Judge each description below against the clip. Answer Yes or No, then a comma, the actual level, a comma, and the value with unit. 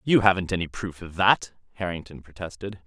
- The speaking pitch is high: No, very low, 90 Hz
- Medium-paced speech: Yes, average, 170 wpm